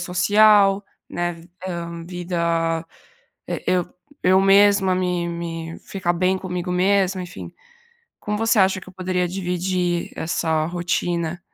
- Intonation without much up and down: Yes, narrow, 1.7 semitones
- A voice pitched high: No, medium, 180 Hz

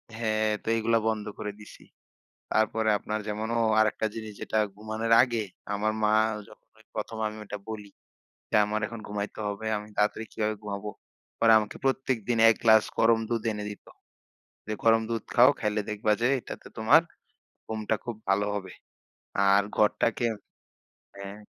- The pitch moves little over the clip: Yes, narrow, 1.2 semitones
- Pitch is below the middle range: Yes, low, 110 Hz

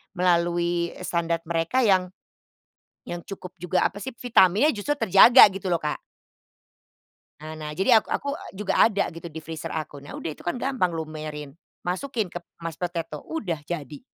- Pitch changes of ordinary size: Yes, average, 3.6 semitones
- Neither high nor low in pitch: Yes, medium, 175 Hz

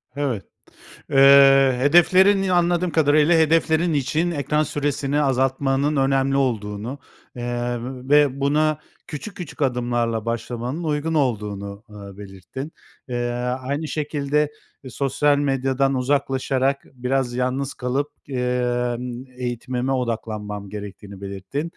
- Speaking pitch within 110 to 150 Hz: Yes, low, 135 Hz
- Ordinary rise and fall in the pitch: Yes, average, 3.3 semitones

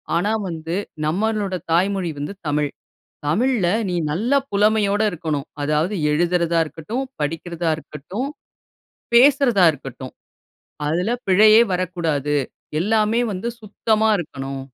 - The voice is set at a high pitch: No, medium, 180 Hz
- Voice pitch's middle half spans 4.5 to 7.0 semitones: Yes, wide, 5.5 semitones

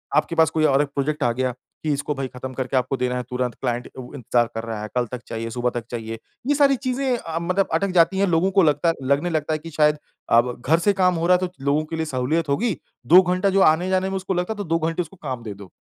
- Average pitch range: No, wide, 6.1 semitones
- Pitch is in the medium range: Yes, medium, 155 Hz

